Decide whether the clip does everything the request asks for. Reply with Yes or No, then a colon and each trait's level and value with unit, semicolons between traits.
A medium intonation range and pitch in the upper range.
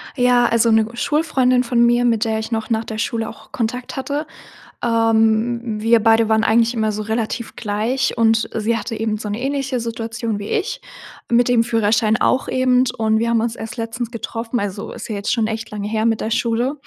No: narrow, 1.7 semitones; high, 230 Hz